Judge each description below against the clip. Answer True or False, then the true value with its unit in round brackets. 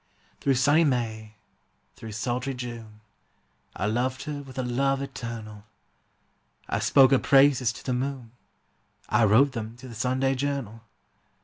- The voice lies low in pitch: True (125 Hz)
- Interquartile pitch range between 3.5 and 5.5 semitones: False (3.0 semitones)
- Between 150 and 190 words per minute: False (140 wpm)